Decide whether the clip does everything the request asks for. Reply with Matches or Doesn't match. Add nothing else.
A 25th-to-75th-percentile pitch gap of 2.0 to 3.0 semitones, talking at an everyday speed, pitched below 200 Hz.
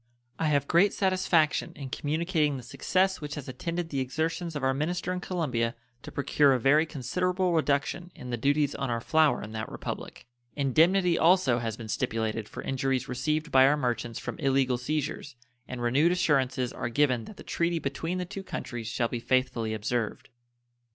Doesn't match